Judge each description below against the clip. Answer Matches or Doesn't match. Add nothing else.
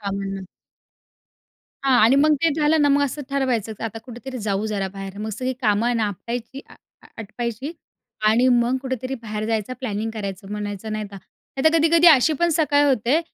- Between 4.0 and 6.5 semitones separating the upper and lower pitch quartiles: Matches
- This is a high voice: Matches